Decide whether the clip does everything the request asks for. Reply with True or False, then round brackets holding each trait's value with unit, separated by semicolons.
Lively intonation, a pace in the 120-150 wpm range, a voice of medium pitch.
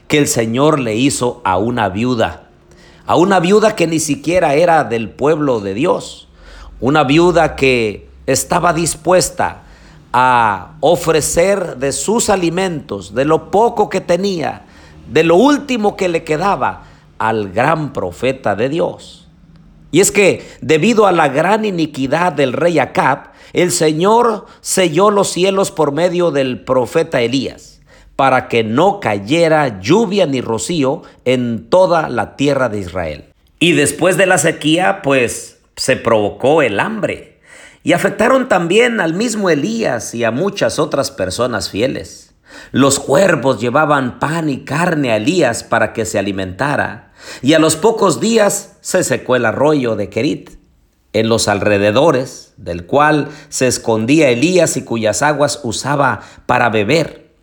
True (6.8 semitones; 145 wpm; 150 Hz)